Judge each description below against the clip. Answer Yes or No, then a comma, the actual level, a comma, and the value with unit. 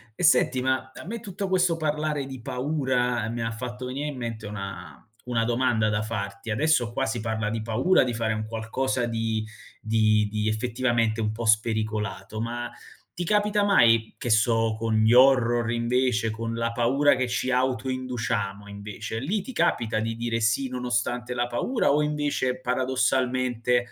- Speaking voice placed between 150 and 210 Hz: No, low, 120 Hz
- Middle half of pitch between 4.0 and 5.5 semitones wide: No, average, 2.7 semitones